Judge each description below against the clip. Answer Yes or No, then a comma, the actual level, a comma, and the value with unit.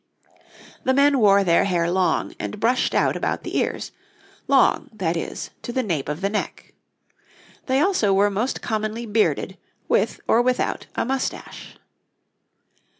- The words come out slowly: No, average, 150 wpm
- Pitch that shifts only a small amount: No, average, 4.6 semitones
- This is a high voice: Yes, high, 215 Hz